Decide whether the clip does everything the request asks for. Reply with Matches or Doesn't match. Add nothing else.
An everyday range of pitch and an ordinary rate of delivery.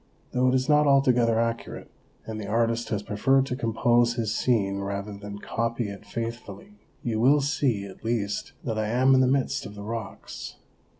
Matches